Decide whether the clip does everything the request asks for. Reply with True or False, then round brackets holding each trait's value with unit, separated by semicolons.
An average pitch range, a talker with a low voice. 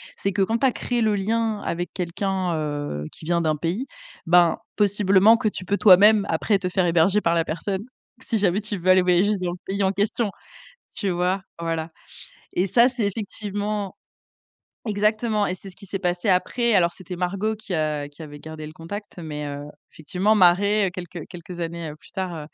False (3.4 semitones; 185 Hz)